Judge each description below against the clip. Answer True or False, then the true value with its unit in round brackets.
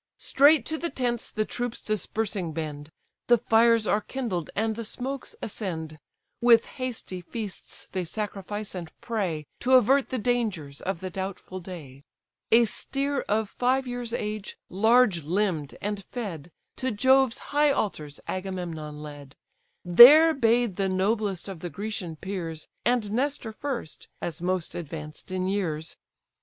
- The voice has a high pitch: True (205 Hz)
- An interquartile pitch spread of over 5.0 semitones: True (5.5 semitones)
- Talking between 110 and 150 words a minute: True (145 wpm)